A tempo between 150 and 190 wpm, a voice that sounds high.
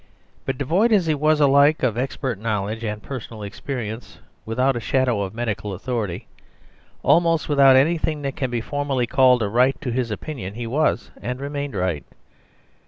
No: average, 170 wpm; low, 125 Hz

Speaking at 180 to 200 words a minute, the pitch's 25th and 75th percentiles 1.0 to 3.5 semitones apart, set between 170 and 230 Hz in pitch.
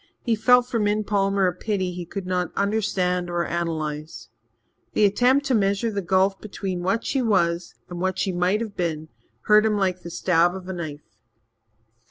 Yes: average, 185 wpm; average, 3.1 semitones; high, 190 Hz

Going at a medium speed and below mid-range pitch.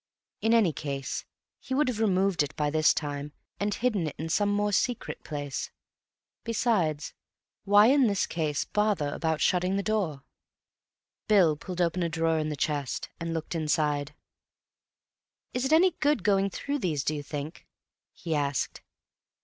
No: average, 160 wpm; medium, 170 Hz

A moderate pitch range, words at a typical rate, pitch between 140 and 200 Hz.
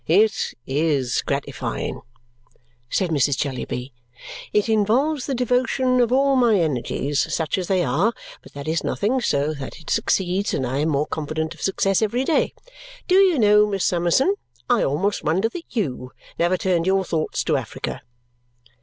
No: wide, 7.3 semitones; average, 165 wpm; medium, 185 Hz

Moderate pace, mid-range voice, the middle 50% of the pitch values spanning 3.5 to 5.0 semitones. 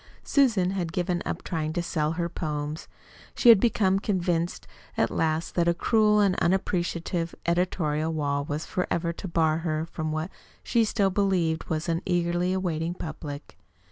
No: average, 160 wpm; medium, 170 Hz; average, 2.8 semitones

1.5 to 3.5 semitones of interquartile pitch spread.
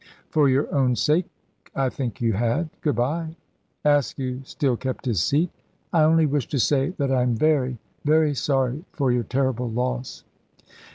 Yes: average, 3.2 semitones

